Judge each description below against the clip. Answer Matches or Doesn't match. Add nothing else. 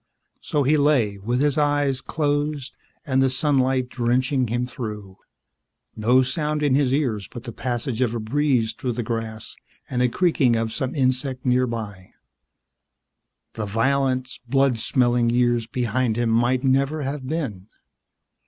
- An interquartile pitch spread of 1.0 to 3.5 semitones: Matches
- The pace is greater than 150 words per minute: Doesn't match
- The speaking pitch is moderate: Doesn't match